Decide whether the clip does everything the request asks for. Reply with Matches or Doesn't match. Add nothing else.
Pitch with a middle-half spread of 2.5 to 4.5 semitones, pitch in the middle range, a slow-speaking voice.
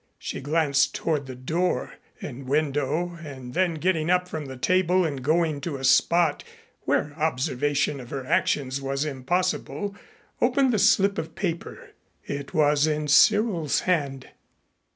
Doesn't match